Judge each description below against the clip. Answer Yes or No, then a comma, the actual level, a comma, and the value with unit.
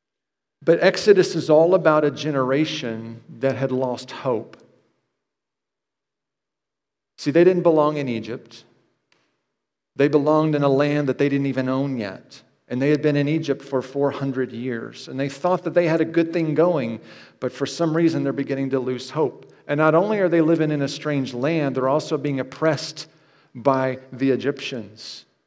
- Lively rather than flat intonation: No, average, 3.1 semitones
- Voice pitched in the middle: Yes, medium, 145 Hz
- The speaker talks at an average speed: Yes, average, 170 wpm